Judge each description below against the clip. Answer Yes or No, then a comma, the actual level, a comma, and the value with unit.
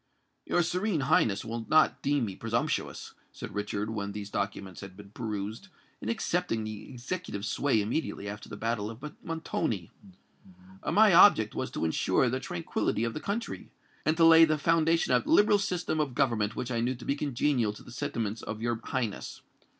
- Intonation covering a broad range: Yes, wide, 6.9 semitones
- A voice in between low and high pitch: No, low, 120 Hz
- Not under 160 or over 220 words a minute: Yes, average, 180 wpm